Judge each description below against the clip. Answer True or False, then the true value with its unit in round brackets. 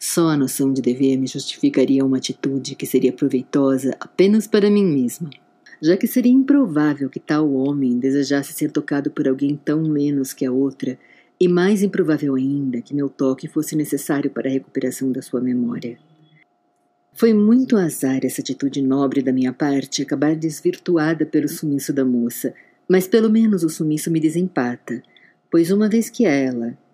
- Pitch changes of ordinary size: True (4.1 semitones)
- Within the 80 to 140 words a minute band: False (165 wpm)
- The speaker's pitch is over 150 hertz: False (145 Hz)